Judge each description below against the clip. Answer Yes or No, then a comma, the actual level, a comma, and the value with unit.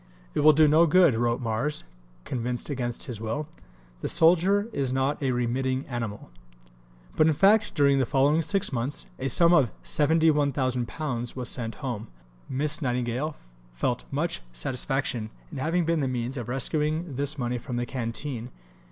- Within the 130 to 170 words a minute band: Yes, average, 160 wpm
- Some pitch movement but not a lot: Yes, average, 3.9 semitones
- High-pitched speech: No, low, 135 Hz